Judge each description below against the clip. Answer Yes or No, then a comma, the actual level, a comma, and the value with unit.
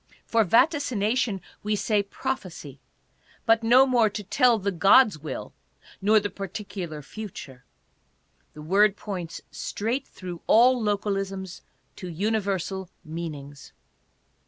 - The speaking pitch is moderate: No, high, 200 Hz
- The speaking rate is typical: No, slow, 115 wpm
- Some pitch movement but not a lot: Yes, average, 4.0 semitones